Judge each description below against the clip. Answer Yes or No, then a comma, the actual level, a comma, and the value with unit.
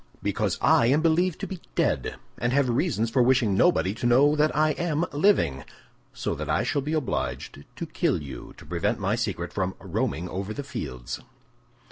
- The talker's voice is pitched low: Yes, low, 120 Hz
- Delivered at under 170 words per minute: No, average, 180 wpm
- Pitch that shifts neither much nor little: No, wide, 7.9 semitones